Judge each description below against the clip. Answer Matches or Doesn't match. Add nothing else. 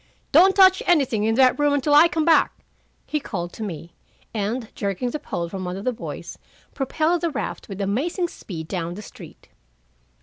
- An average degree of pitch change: Doesn't match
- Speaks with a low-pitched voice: Doesn't match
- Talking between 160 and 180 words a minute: Doesn't match